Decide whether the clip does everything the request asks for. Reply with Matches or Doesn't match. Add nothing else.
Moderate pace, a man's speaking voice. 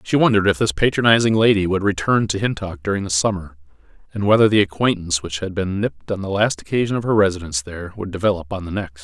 Doesn't match